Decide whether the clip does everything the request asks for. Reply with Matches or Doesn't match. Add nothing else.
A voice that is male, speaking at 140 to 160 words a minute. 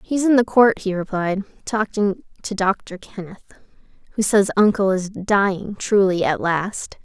Doesn't match